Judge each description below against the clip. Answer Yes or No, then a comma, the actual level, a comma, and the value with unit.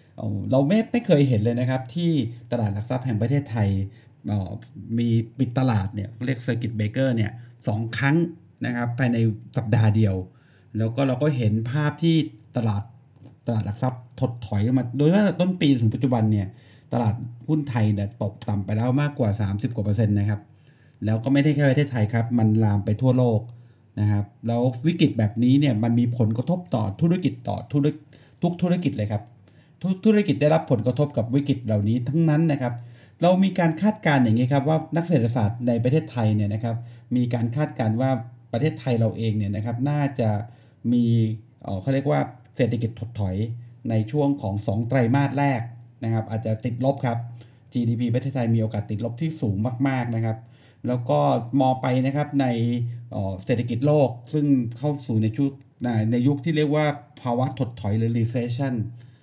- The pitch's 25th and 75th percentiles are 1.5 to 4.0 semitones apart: Yes, average, 3.7 semitones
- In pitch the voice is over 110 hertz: Yes, low, 120 Hz